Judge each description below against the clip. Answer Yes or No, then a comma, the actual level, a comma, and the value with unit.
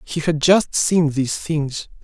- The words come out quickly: No, average, 175 wpm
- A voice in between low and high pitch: Yes, medium, 155 Hz